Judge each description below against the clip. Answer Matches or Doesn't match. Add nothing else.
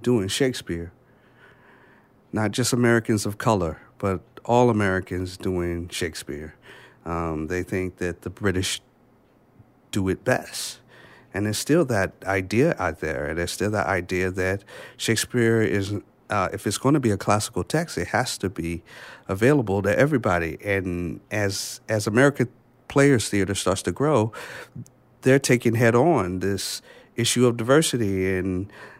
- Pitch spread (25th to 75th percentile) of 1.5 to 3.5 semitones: Doesn't match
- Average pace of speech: Matches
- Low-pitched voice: Matches